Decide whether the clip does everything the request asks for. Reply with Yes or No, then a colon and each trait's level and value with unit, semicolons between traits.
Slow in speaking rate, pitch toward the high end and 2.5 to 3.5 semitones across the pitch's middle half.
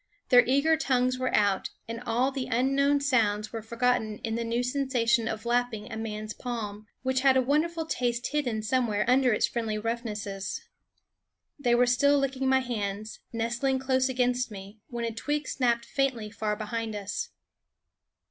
No: average, 165 wpm; high, 240 Hz; average, 3.0 semitones